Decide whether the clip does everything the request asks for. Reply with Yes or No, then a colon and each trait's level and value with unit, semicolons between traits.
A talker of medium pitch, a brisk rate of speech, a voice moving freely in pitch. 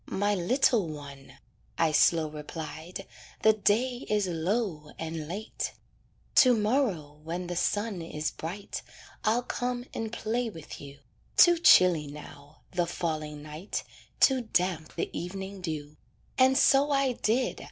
No: medium, 180 Hz; slow, 135 wpm; wide, 6.4 semitones